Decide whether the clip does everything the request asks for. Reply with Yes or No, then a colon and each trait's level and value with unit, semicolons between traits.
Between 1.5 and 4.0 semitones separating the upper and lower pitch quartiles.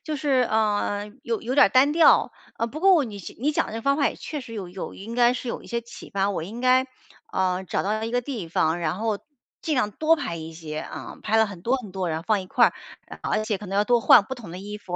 No: average, 4.7 semitones